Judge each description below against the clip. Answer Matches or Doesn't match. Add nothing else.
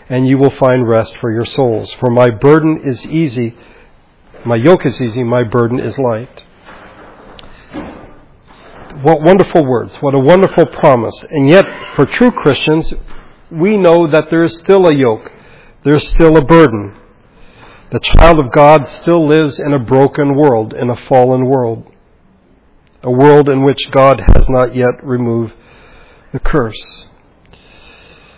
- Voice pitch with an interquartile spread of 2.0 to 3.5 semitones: Doesn't match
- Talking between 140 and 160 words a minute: Matches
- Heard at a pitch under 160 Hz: Matches